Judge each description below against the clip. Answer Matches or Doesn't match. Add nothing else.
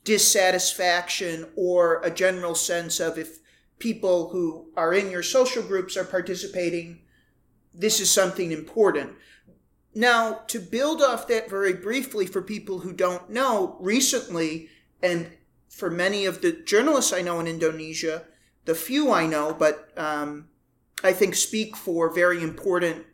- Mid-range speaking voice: Matches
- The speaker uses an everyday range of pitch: Matches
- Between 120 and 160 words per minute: Matches